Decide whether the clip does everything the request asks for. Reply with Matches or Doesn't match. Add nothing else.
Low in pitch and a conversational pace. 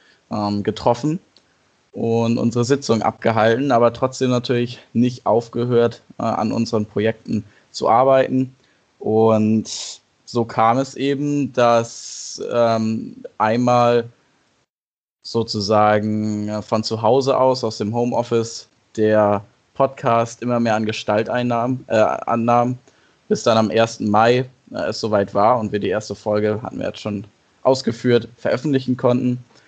Doesn't match